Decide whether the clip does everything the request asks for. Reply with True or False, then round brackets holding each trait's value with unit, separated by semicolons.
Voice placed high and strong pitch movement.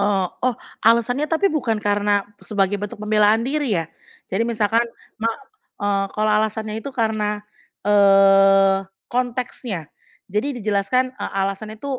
False (210 Hz; 2.8 semitones)